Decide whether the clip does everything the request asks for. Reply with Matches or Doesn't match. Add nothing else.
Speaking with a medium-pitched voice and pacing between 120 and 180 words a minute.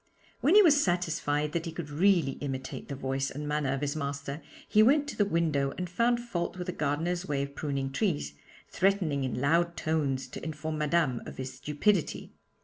Doesn't match